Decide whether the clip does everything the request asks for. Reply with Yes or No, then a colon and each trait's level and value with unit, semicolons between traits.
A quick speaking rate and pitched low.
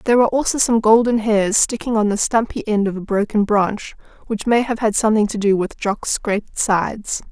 No: fast, 215 wpm; high, 215 Hz